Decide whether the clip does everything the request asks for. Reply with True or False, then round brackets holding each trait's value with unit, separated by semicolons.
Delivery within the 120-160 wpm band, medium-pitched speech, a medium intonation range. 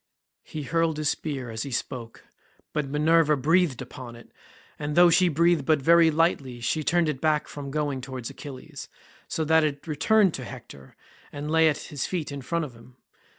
False (190 wpm; 150 Hz; 3.5 semitones)